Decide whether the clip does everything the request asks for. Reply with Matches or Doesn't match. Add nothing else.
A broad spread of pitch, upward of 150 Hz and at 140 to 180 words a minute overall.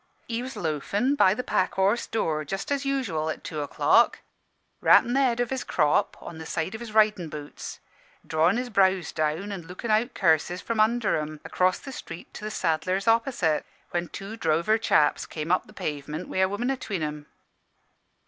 Doesn't match